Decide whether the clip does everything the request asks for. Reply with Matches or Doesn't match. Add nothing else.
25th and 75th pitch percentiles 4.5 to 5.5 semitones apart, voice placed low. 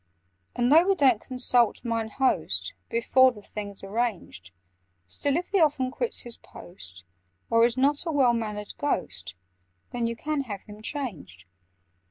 Doesn't match